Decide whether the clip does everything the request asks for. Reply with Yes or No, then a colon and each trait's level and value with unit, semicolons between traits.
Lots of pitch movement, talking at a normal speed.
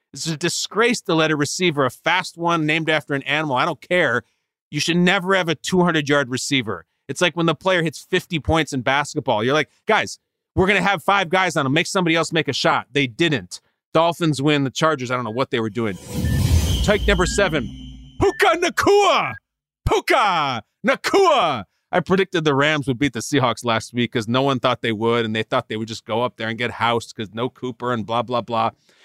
No: wide, 5.9 semitones; fast, 220 wpm